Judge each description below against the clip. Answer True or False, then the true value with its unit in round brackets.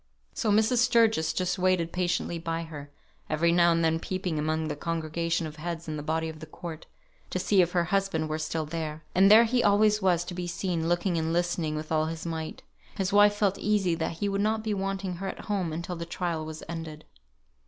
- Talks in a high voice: False (170 Hz)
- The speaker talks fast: True (220 wpm)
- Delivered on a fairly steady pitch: False (3.2 semitones)